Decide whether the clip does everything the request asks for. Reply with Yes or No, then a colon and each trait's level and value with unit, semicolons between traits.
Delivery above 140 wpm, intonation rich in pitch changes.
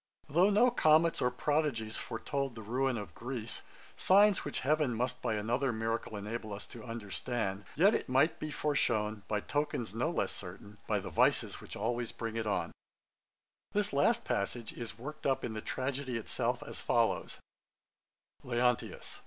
No: average, 160 wpm; average, 4.8 semitones